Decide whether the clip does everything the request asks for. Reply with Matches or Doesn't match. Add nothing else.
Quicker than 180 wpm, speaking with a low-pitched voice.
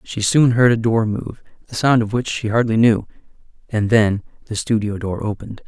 Matches